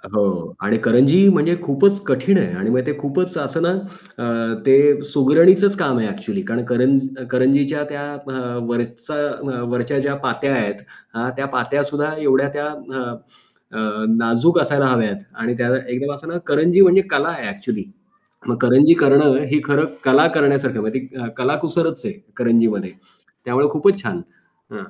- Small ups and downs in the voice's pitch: No, average, 4.4 semitones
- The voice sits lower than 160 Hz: Yes, medium, 140 Hz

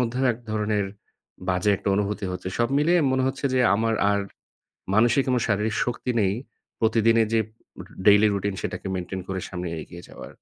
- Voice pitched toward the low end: Yes, low, 105 Hz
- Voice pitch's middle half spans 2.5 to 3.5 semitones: Yes, average, 2.9 semitones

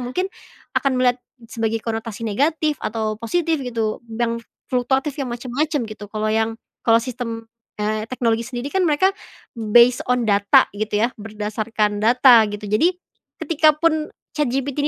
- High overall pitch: Yes, high, 235 Hz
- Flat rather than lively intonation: No, average, 3.8 semitones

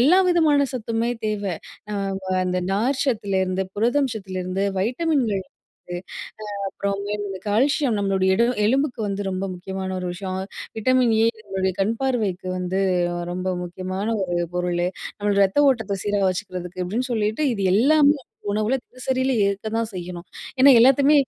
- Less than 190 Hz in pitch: No, high, 205 Hz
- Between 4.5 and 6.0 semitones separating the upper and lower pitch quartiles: Yes, average, 5.1 semitones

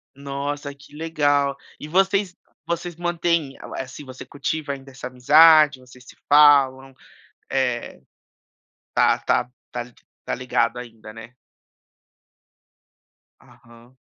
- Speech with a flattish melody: No, average, 3.2 semitones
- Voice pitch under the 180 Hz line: Yes, medium, 140 Hz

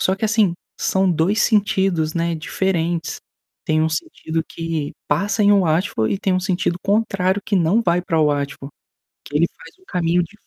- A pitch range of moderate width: Yes, average, 3.4 semitones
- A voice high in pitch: No, medium, 175 Hz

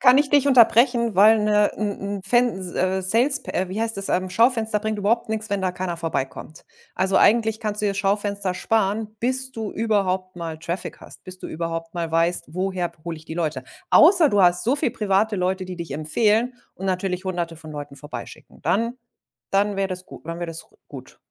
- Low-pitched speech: No, high, 195 Hz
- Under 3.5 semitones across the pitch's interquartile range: No, average, 3.8 semitones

